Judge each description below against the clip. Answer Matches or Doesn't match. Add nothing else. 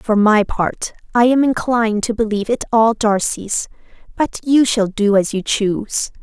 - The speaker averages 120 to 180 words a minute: Matches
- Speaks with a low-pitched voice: Doesn't match